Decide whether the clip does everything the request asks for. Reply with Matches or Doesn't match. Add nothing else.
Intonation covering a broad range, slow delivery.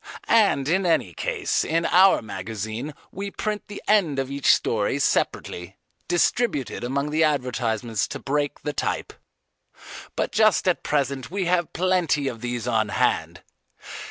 Doesn't match